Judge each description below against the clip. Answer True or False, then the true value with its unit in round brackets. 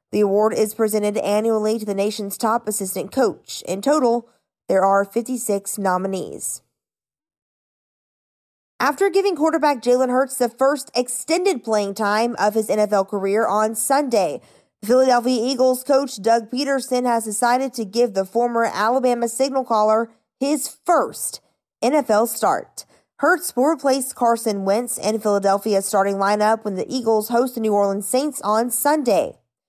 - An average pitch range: True (3.5 semitones)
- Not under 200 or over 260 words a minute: False (140 wpm)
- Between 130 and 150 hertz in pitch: False (230 Hz)